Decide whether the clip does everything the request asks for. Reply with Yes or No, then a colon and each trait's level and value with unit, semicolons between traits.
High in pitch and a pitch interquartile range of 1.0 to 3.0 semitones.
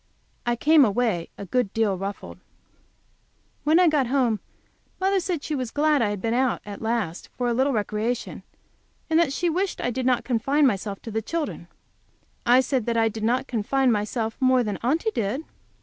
No: high, 245 Hz; average, 4.3 semitones